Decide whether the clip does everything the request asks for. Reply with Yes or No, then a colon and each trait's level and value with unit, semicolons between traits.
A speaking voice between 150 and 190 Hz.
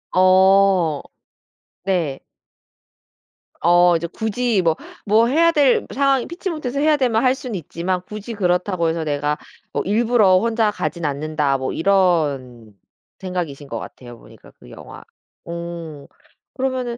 Yes: medium, 185 Hz